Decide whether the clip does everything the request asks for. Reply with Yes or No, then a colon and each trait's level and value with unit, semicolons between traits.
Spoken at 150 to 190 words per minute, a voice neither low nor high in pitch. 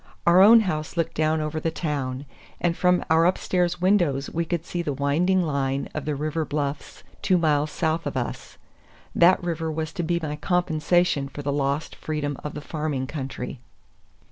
Yes: average, 180 wpm; medium, 155 Hz